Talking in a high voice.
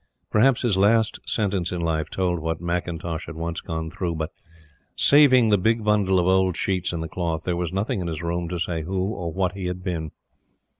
No: very low, 90 Hz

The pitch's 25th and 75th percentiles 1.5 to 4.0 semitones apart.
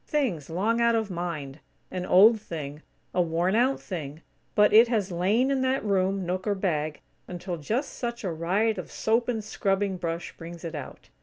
No: average, 4.8 semitones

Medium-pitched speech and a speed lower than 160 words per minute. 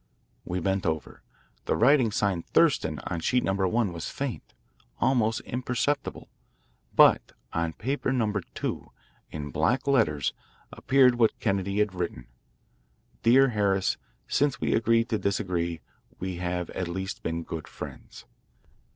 No: low, 100 Hz; slow, 135 wpm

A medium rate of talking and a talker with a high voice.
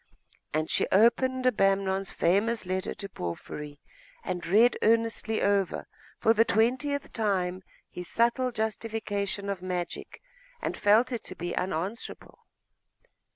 No: slow, 120 wpm; high, 205 Hz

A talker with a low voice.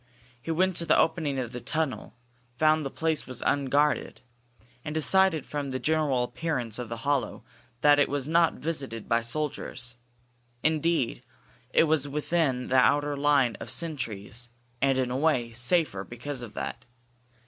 No: medium, 145 Hz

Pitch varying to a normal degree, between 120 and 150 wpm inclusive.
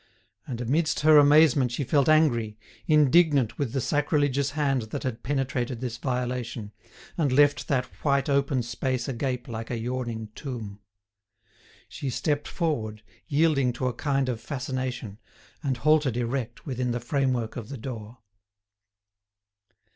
Yes: average, 3.2 semitones; average, 140 wpm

